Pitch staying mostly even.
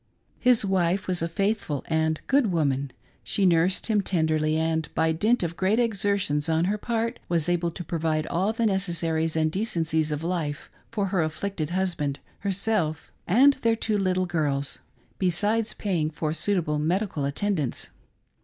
No: average, 4.1 semitones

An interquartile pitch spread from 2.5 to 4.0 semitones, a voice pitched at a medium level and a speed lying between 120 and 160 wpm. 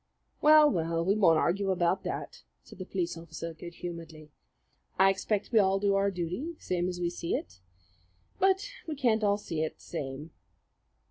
No: average, 3.4 semitones; medium, 180 Hz; average, 180 wpm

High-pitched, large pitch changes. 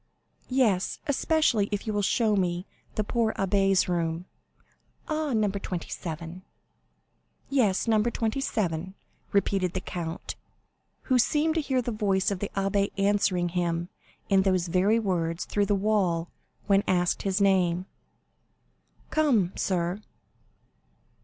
No: high, 195 Hz; average, 3.3 semitones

